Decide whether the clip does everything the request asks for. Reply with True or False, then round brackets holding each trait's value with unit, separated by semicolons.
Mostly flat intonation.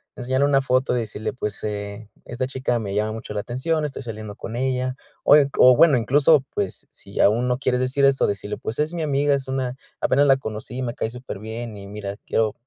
False (3.7 semitones)